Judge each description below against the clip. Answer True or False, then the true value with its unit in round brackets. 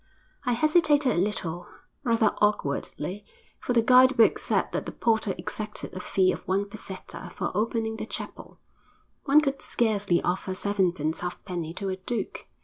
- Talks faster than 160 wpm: False (155 wpm)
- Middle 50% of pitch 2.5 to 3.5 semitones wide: False (4.0 semitones)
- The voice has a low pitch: False (210 Hz)